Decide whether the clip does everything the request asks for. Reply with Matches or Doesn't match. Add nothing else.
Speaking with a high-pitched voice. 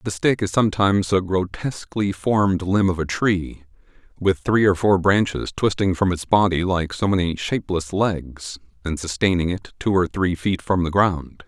Doesn't match